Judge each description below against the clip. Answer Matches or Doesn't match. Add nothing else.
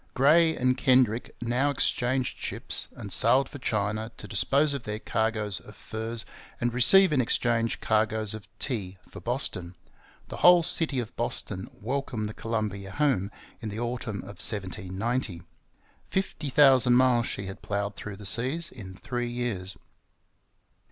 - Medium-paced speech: Matches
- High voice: Doesn't match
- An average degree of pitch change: Matches